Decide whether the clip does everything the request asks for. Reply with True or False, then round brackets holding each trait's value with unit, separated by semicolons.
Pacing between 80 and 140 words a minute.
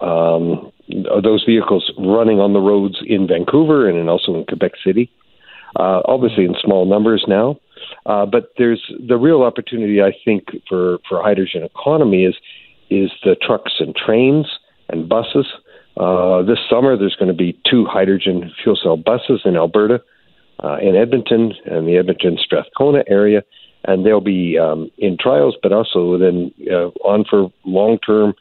False (160 wpm)